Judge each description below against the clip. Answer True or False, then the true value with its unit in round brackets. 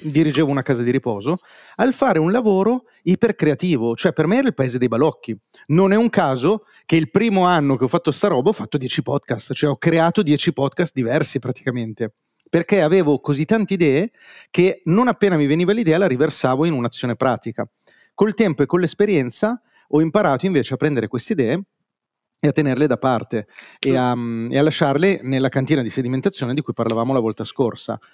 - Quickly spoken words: True (190 wpm)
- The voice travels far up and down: True (6.4 semitones)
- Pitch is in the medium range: True (155 Hz)